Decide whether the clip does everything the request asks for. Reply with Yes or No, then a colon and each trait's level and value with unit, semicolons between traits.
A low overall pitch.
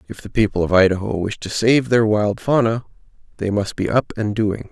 Yes: low, 105 Hz